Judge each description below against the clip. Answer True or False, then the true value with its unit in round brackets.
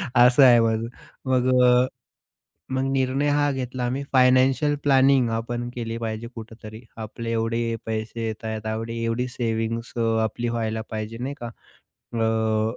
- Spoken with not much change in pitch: True (2.2 semitones)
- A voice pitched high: False (115 Hz)